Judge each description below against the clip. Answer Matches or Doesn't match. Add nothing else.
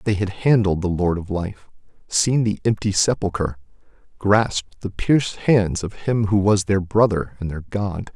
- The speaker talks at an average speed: Matches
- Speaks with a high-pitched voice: Doesn't match